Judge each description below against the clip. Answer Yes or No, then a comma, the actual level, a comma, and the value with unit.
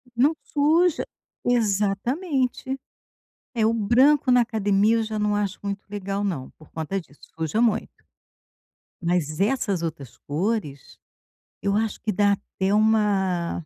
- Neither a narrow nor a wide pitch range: Yes, average, 3.6 semitones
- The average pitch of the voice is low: No, high, 205 Hz